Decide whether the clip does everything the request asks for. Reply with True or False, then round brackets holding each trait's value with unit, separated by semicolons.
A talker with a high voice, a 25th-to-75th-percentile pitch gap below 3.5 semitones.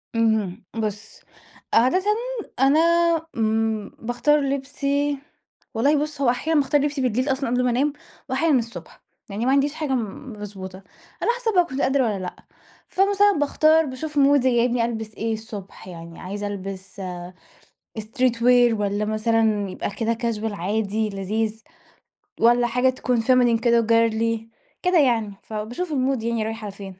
False (235 Hz; 4.2 semitones)